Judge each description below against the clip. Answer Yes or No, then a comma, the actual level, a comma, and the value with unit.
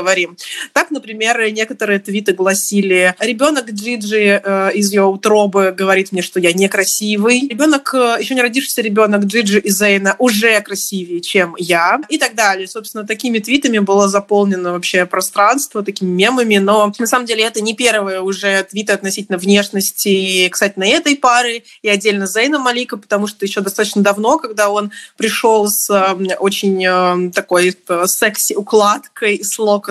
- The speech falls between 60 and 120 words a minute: No, average, 150 wpm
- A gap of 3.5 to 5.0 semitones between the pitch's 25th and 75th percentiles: No, narrow, 2.5 semitones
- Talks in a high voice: Yes, high, 205 Hz